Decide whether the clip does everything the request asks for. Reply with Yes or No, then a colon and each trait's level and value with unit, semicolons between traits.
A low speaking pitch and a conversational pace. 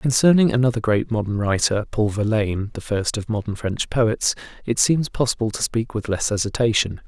Yes: low, 110 Hz; average, 160 wpm